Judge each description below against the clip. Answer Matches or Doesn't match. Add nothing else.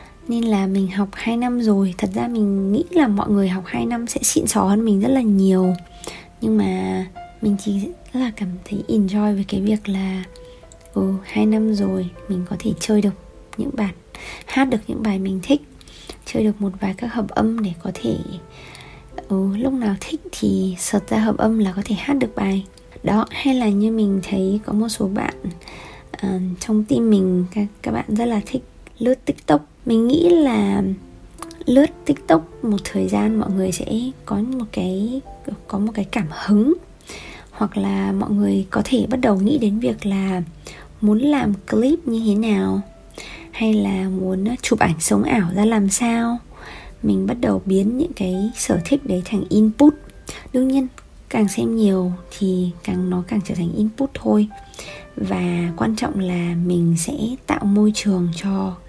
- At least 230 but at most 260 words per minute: Doesn't match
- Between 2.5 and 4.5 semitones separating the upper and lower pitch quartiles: Matches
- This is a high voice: Matches